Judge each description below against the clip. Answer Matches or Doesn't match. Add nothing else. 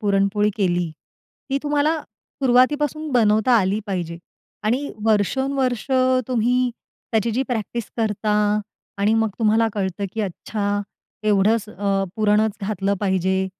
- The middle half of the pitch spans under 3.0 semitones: Doesn't match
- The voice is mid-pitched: Doesn't match